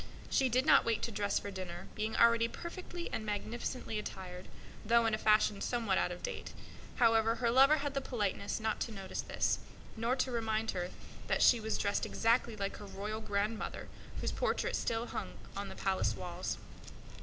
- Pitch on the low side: No, high, 225 Hz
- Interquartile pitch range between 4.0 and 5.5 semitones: No, narrow, 2.6 semitones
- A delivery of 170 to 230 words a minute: Yes, average, 180 wpm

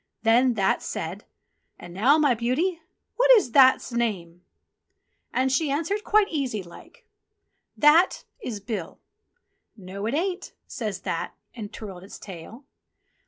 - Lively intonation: Yes, wide, 7.2 semitones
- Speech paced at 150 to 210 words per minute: No, slow, 135 wpm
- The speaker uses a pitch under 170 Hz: No, high, 235 Hz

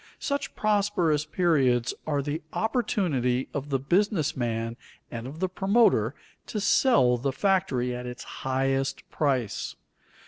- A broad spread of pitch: Yes, wide, 7.1 semitones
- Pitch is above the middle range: No, medium, 140 Hz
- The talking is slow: Yes, slow, 130 wpm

